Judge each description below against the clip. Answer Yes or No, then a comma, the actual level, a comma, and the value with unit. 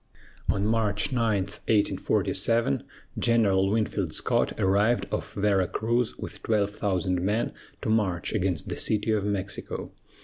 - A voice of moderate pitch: No, low, 105 Hz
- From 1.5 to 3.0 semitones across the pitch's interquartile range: Yes, narrow, 2.5 semitones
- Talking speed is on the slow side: Yes, slow, 130 wpm